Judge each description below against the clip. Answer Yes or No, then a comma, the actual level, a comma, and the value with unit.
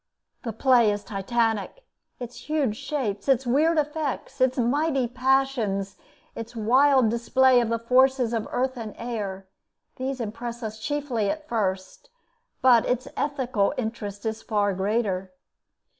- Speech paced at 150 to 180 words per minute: No, slow, 135 wpm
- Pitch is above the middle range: Yes, high, 240 Hz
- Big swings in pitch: No, average, 3.6 semitones